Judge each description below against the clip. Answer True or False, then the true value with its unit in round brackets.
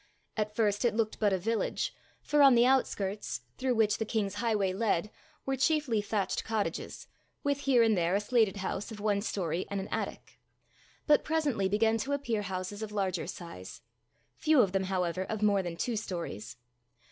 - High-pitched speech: True (210 Hz)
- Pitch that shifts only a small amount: False (3.4 semitones)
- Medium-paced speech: True (180 wpm)